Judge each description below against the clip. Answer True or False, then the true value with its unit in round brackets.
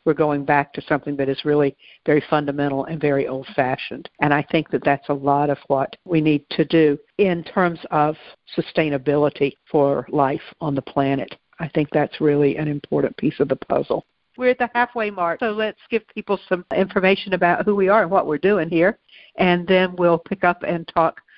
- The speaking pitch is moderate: True (165 Hz)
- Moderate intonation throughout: True (4.6 semitones)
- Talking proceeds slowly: False (205 wpm)